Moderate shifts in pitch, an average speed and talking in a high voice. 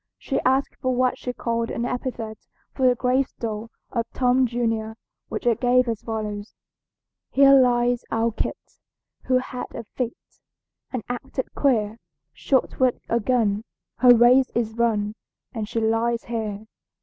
No: narrow, 2.1 semitones; average, 150 wpm; high, 235 Hz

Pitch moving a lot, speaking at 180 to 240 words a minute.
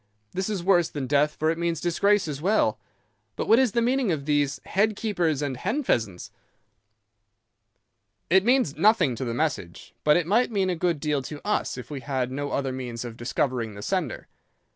Yes: wide, 6.4 semitones; average, 195 wpm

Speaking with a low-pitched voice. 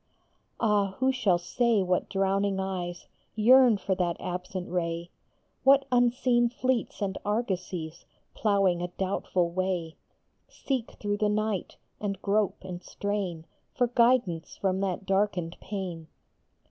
No: high, 195 Hz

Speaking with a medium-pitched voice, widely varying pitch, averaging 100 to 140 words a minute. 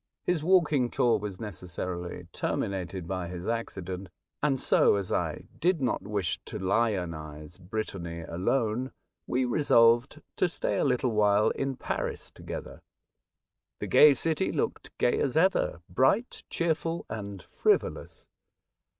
No: low, 110 Hz; wide, 6.9 semitones; slow, 135 wpm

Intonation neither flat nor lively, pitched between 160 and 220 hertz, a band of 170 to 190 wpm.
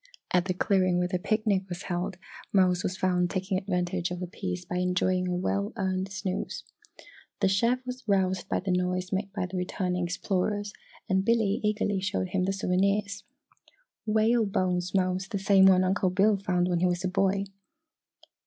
No: narrow, 1.7 semitones; medium, 185 Hz; average, 180 wpm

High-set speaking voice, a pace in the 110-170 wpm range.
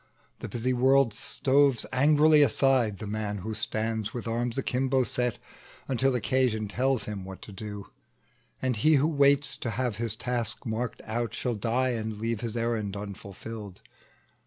No: low, 115 Hz; average, 160 wpm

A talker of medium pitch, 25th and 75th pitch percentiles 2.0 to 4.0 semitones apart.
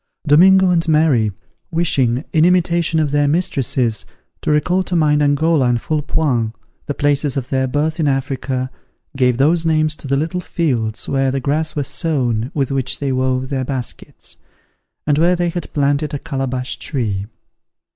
Yes: medium, 145 Hz; average, 3.5 semitones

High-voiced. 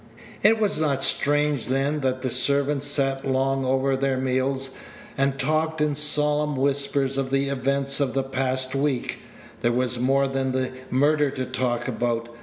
No: low, 135 Hz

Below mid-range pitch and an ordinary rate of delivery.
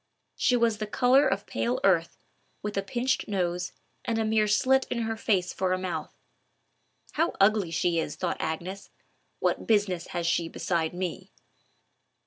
No: high, 200 Hz; average, 160 wpm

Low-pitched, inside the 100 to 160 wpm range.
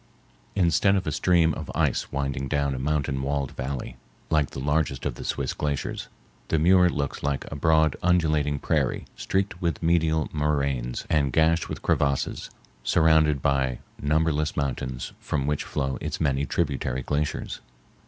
Yes: very low, 75 Hz; average, 155 wpm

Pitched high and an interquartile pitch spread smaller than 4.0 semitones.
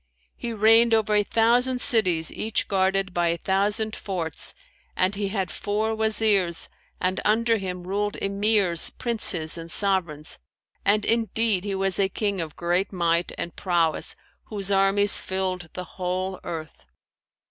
Yes: high, 195 Hz; average, 3.1 semitones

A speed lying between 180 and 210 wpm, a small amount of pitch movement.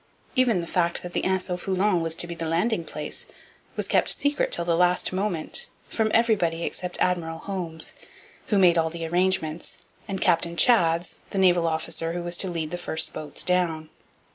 Yes: average, 190 wpm; narrow, 2.3 semitones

